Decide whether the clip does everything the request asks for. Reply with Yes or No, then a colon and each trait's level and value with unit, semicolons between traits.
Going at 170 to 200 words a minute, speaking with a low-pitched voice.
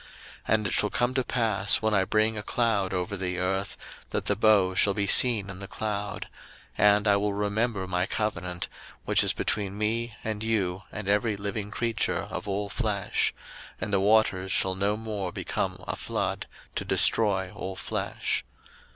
Yes: average, 180 wpm; low, 105 Hz